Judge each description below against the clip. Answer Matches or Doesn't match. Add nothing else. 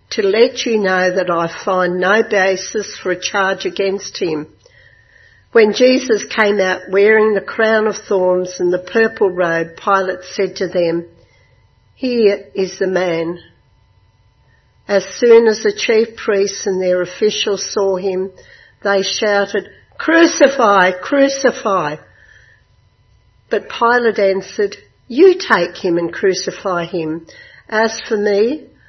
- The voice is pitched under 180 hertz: Doesn't match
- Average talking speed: Doesn't match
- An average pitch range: Matches